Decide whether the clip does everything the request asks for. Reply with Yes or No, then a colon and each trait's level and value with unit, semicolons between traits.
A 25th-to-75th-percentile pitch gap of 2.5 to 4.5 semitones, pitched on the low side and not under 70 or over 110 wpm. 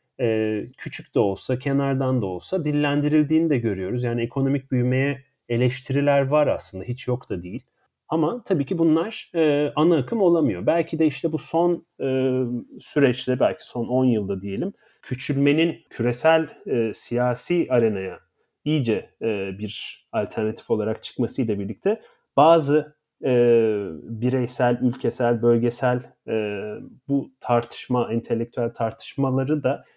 No: average, 4.1 semitones; low, 130 Hz; average, 125 wpm